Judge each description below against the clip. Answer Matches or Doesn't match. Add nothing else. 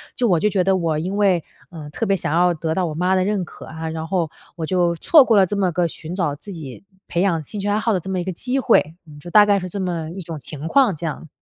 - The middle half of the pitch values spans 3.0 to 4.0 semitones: Matches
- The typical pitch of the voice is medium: Matches